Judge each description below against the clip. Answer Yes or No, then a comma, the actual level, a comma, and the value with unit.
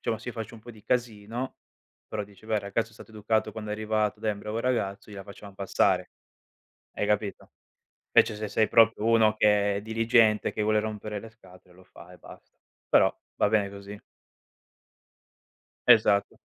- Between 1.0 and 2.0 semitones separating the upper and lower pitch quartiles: Yes, narrow, 1.6 semitones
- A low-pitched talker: Yes, low, 105 Hz